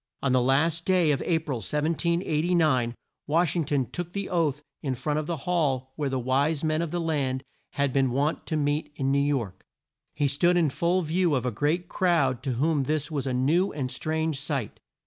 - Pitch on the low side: No, medium, 150 Hz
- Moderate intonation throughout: Yes, average, 3.7 semitones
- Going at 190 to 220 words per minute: Yes, fast, 205 wpm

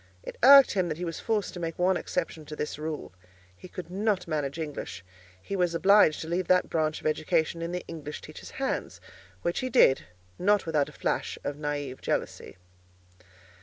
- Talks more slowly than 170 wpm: No, average, 190 wpm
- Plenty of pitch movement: No, average, 3.3 semitones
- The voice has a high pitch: No, medium, 165 Hz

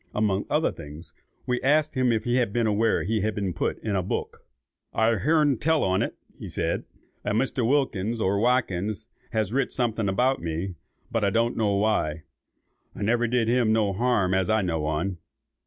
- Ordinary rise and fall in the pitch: Yes, average, 4.0 semitones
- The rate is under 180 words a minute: No, average, 190 wpm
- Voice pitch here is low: Yes, low, 110 Hz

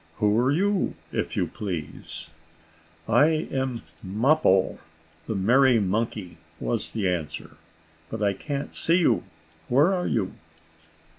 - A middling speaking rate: No, slow, 125 wpm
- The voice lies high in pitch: No, low, 115 Hz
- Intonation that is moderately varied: No, wide, 6.4 semitones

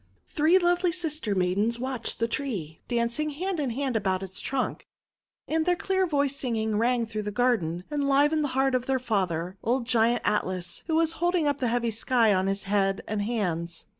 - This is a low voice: No, high, 240 Hz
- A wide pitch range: Yes, wide, 6.0 semitones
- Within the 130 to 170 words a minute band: No, average, 195 wpm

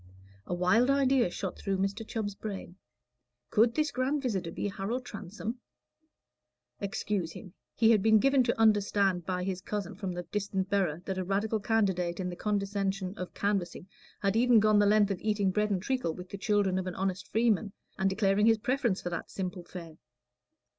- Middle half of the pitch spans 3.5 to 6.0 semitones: No, average, 2.9 semitones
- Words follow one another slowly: No, average, 185 wpm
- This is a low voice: No, high, 200 Hz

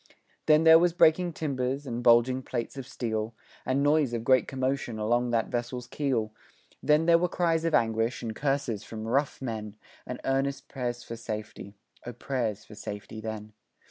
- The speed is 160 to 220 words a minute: Yes, average, 175 wpm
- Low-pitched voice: Yes, low, 125 Hz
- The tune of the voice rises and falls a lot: No, average, 3.7 semitones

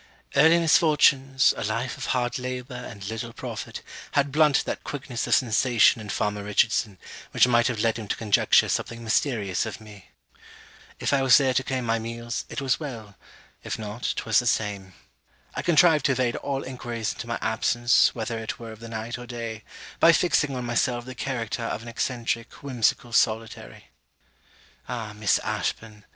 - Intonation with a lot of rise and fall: No, average, 2.9 semitones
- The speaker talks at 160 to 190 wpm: Yes, average, 175 wpm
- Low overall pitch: Yes, low, 120 Hz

